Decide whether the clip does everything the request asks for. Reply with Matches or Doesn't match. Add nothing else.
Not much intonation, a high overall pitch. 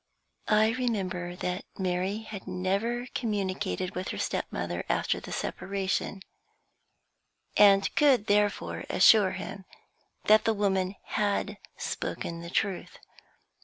Matches